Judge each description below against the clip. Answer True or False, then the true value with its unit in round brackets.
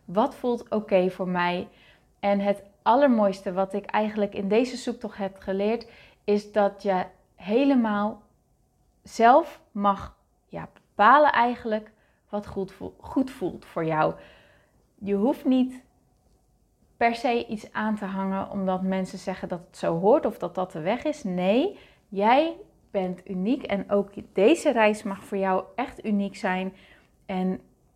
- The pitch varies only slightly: False (3.5 semitones)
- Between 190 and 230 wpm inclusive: False (150 wpm)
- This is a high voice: True (205 Hz)